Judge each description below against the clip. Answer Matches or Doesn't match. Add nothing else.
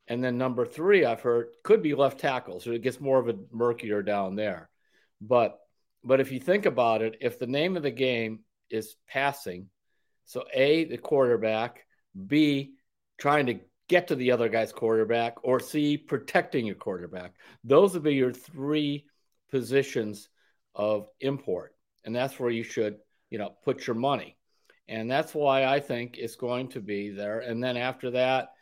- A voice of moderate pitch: Doesn't match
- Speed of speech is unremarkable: Matches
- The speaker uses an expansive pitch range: Doesn't match